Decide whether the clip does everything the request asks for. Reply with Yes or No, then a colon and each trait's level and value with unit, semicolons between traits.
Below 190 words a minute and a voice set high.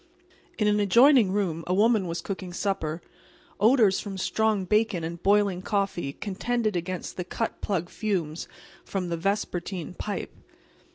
Yes: average, 140 wpm; high, 195 Hz